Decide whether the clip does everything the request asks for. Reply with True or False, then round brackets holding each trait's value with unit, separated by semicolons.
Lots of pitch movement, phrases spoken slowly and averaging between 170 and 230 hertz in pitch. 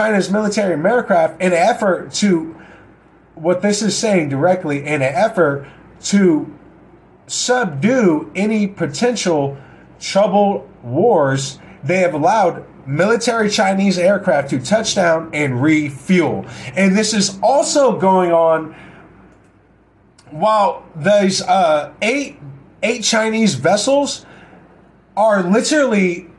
False (5.0 semitones; 105 wpm; 185 Hz)